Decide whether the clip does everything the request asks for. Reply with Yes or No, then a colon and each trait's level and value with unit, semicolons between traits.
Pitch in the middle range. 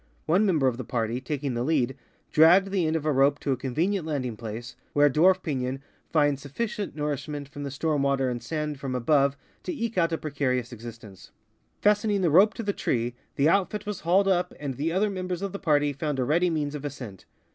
Yes: medium, 145 Hz